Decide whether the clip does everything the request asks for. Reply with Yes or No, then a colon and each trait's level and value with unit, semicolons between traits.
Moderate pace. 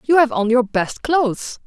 No: fast, 215 wpm